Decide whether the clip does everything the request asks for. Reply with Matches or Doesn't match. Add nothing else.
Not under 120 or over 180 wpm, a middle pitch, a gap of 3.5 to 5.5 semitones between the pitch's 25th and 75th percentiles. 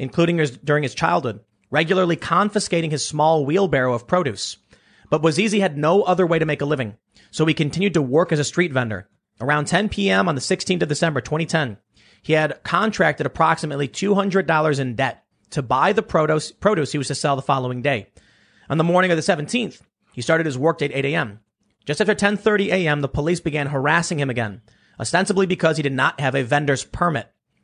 Doesn't match